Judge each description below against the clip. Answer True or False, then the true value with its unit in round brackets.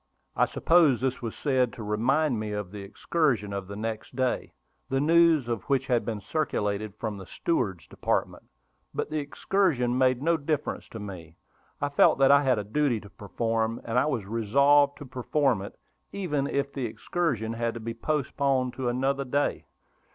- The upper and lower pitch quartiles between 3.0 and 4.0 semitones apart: False (4.6 semitones)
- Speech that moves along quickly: False (180 wpm)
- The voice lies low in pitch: True (125 Hz)